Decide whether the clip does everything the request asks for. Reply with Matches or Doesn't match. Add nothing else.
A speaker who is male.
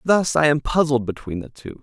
Matches